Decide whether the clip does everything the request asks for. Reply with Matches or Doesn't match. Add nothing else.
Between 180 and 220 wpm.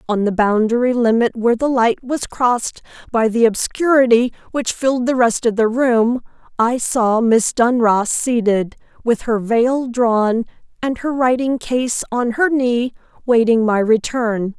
Doesn't match